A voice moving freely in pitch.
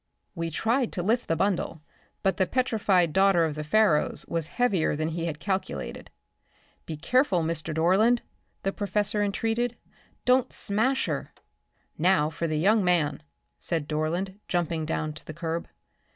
No: average, 4.8 semitones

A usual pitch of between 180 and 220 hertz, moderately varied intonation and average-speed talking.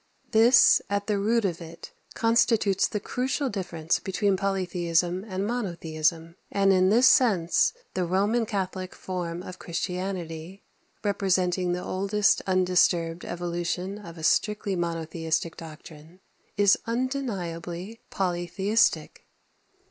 No: medium, 185 Hz; average, 3.1 semitones; slow, 110 wpm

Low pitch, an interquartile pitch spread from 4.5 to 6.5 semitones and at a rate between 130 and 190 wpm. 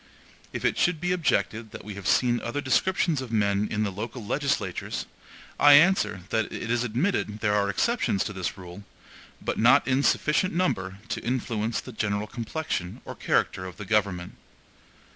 Yes: low, 115 Hz; wide, 5.4 semitones; average, 175 wpm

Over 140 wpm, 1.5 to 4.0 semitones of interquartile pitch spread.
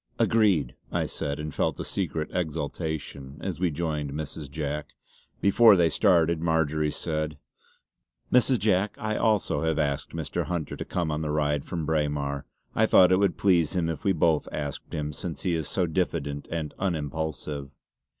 Yes: average, 170 wpm; average, 3.2 semitones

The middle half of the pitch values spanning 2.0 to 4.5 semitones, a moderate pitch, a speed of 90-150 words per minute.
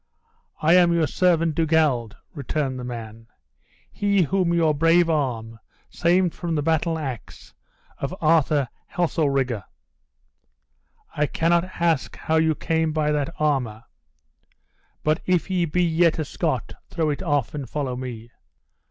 Yes: average, 3.7 semitones; medium, 155 Hz; average, 140 wpm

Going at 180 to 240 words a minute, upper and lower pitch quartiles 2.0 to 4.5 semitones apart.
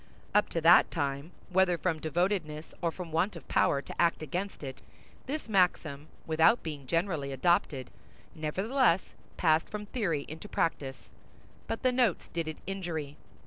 No: average, 150 wpm; average, 3.9 semitones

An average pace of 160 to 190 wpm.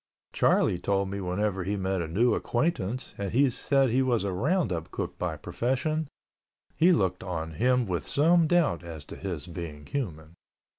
Yes: average, 170 wpm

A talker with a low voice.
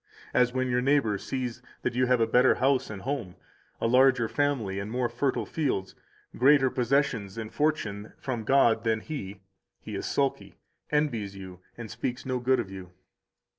Yes: low, 125 Hz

